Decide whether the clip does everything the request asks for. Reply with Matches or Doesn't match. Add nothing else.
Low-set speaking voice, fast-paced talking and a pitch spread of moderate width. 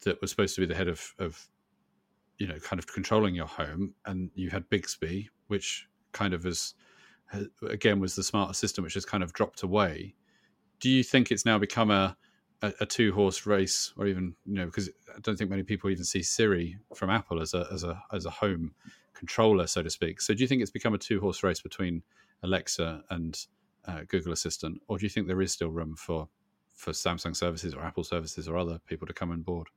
Matches